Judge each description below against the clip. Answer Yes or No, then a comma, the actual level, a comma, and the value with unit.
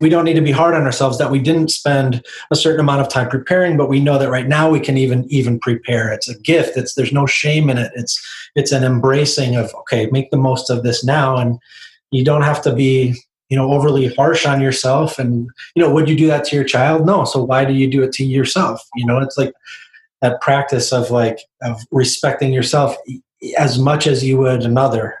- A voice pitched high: No, low, 135 Hz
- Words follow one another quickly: Yes, fast, 235 wpm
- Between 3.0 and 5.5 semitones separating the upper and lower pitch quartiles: No, narrow, 2.4 semitones